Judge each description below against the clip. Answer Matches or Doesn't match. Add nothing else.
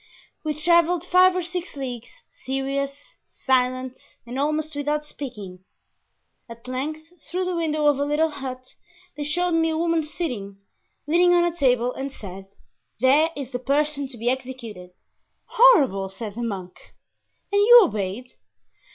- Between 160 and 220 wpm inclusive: Doesn't match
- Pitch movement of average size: Matches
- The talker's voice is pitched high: Matches